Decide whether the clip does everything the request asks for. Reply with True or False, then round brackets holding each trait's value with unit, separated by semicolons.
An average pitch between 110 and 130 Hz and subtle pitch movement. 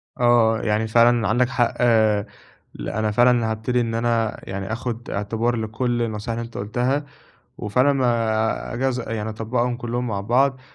True (115 Hz; 1.9 semitones)